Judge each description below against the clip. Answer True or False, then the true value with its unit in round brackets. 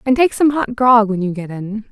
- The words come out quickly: True (285 wpm)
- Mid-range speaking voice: False (225 Hz)